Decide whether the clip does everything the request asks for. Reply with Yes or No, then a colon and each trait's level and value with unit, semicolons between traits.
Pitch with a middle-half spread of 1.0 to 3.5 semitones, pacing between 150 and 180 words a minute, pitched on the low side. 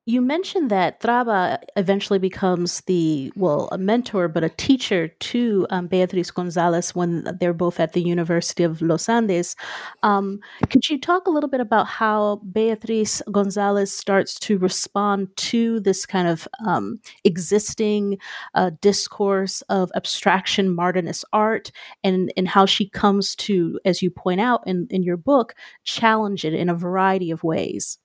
No: average, 3.2 semitones; average, 155 wpm; high, 195 Hz